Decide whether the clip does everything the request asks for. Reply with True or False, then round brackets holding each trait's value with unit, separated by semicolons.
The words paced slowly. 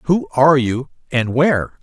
True (130 wpm)